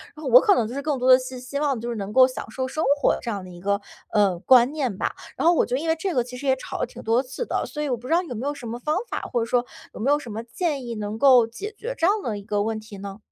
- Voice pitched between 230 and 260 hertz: Yes, very high, 250 Hz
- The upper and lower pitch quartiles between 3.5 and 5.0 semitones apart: Yes, average, 4.4 semitones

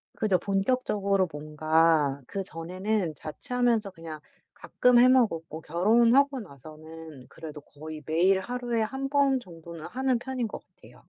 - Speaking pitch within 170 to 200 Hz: Yes, high, 190 Hz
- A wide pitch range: Yes, wide, 7.3 semitones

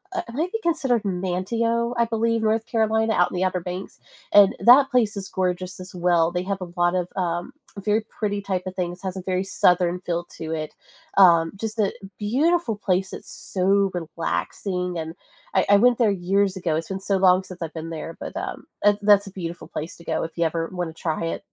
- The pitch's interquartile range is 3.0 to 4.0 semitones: Yes, average, 3.3 semitones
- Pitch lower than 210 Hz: Yes, medium, 185 Hz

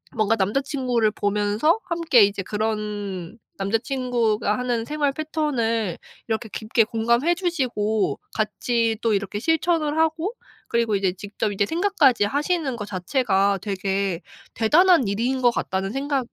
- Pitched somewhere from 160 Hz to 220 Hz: No, high, 230 Hz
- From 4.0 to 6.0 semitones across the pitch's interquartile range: Yes, average, 5.3 semitones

